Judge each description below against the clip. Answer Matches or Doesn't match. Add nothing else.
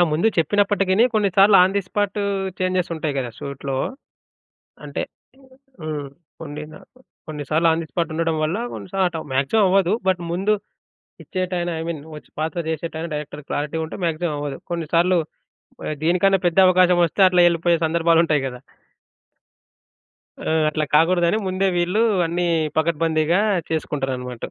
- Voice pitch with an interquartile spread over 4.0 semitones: Doesn't match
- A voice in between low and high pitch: Matches